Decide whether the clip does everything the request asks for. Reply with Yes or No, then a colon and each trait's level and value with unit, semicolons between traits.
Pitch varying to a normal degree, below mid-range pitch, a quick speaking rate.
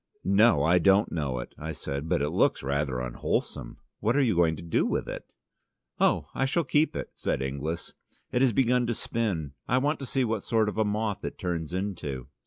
No: wide, 7.8 semitones; very low, 95 Hz; fast, 210 wpm